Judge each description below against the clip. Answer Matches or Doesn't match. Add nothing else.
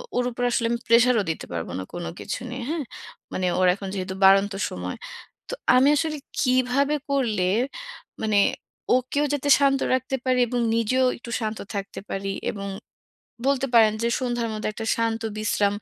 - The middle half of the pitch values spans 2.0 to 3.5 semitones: Doesn't match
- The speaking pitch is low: Doesn't match